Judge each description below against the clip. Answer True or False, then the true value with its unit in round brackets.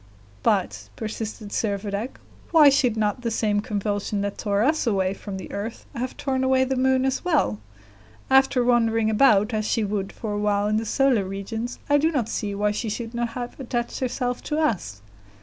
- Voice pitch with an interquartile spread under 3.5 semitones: False (3.9 semitones)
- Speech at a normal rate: True (190 wpm)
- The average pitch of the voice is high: True (225 Hz)